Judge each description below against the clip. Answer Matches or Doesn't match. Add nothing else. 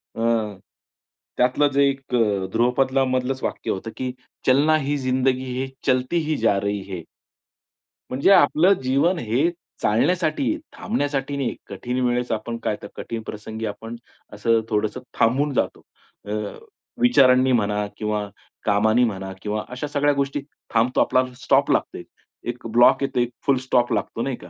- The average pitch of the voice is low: Matches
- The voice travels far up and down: Doesn't match